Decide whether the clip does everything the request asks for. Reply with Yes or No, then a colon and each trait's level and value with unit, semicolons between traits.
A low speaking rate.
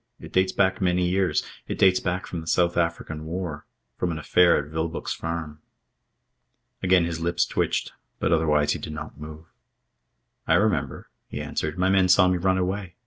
No: average, 180 wpm